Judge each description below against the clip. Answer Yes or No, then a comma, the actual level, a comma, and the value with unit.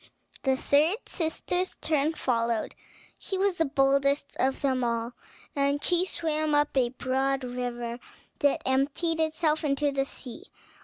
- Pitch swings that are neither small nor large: Yes, average, 3.3 semitones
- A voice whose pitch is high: Yes, very high, 280 Hz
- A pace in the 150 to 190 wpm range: No, average, 140 wpm